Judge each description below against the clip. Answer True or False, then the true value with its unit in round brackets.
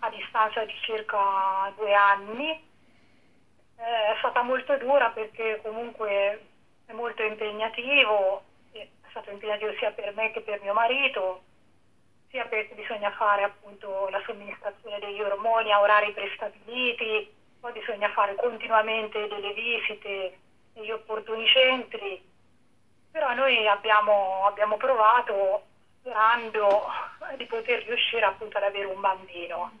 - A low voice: False (215 Hz)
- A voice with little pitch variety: True (2.2 semitones)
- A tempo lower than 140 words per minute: True (120 wpm)